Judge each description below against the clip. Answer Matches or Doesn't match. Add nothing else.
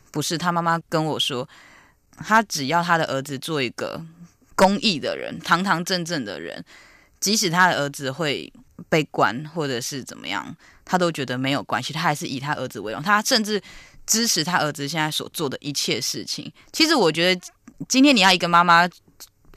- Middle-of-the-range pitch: Matches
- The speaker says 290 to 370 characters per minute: Doesn't match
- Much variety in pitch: Doesn't match